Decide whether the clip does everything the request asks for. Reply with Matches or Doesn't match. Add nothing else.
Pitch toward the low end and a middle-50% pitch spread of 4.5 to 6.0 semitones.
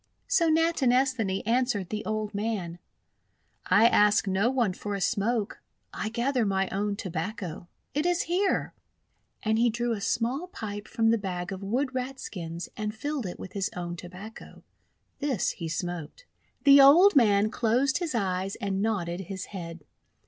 Doesn't match